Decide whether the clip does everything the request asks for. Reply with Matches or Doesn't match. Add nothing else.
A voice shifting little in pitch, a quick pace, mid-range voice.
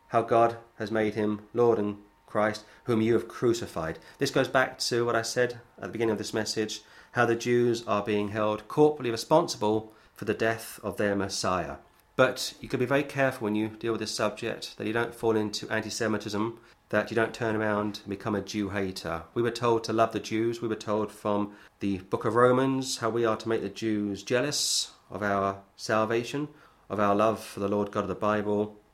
Doesn't match